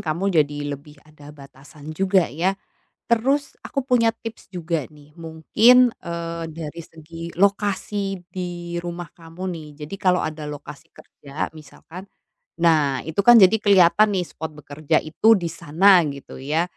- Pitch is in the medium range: Yes, medium, 170 Hz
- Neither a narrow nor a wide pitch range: Yes, average, 4.0 semitones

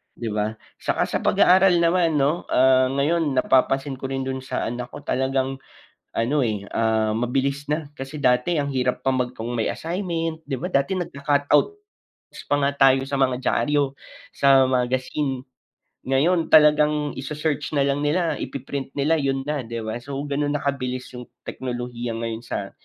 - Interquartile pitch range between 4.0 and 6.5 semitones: No, average, 2.7 semitones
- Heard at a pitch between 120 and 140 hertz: Yes, low, 135 Hz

